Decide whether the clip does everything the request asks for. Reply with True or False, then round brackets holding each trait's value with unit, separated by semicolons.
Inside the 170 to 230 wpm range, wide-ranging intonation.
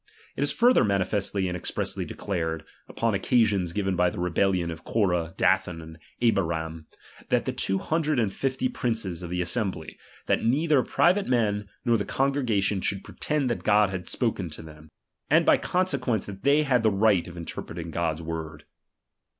True (190 wpm; 5.8 semitones)